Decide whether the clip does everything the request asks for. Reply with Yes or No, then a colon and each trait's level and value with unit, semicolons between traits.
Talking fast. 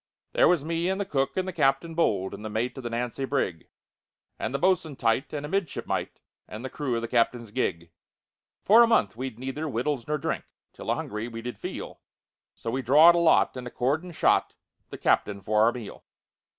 Yes: fast, 210 wpm